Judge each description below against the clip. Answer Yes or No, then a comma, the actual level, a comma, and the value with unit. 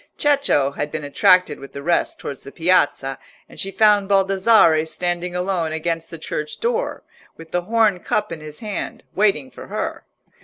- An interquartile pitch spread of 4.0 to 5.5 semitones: Yes, average, 4.5 semitones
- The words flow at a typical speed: Yes, average, 170 wpm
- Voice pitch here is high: No, medium, 175 Hz